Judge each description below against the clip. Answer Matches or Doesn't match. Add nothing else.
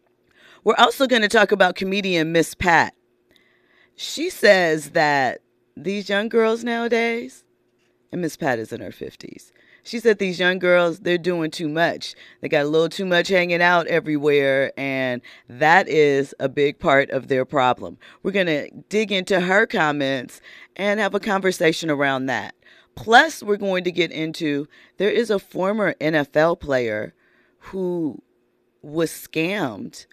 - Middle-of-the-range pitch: Matches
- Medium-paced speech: Matches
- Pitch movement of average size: Matches